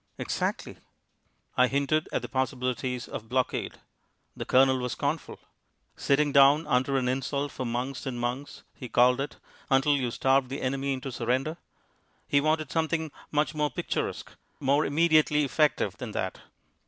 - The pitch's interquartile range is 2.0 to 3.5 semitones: Yes, narrow, 2.6 semitones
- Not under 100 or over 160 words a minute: Yes, average, 150 wpm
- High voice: No, low, 135 Hz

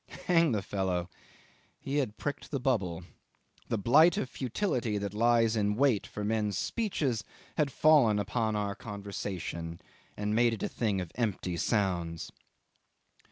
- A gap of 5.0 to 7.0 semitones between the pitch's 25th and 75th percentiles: No, average, 4.1 semitones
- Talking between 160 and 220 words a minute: No, average, 145 wpm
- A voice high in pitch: No, low, 105 Hz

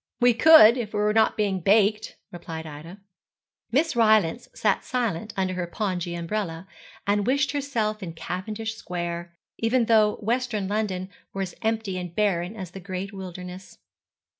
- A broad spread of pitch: No, average, 3.6 semitones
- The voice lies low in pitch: No, high, 205 Hz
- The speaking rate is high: No, average, 155 wpm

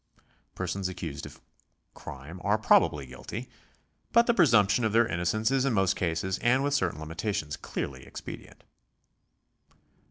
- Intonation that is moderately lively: No, wide, 5.9 semitones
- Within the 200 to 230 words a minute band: No, average, 150 wpm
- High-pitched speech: No, very low, 95 Hz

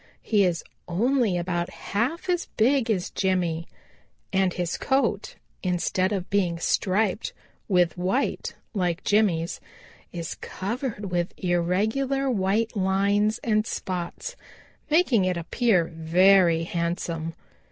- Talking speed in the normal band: No, slow, 110 wpm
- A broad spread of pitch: No, average, 4.0 semitones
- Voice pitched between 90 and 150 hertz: No, high, 190 Hz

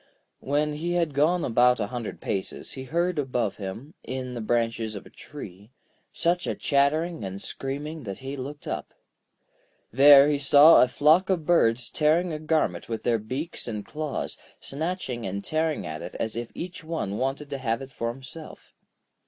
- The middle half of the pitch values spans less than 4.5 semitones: No, average, 5.0 semitones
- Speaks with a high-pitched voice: No, low, 135 Hz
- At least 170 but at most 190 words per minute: Yes, average, 175 wpm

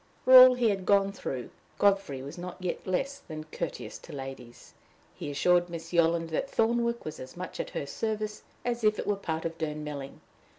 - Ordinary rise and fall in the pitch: No, wide, 5.8 semitones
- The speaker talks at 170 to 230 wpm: Yes, average, 200 wpm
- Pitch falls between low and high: Yes, medium, 175 Hz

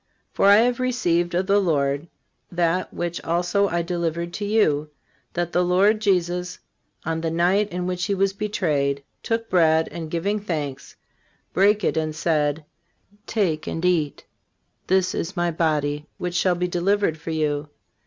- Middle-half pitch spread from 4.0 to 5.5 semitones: No, average, 3.4 semitones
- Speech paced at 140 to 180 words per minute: Yes, average, 160 wpm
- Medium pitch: Yes, medium, 175 Hz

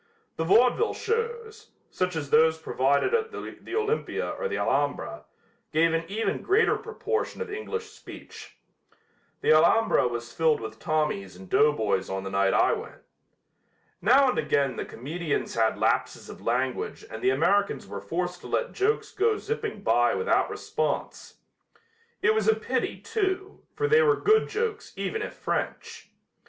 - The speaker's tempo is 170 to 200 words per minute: No, average, 155 wpm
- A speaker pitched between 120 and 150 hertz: No, high, 190 Hz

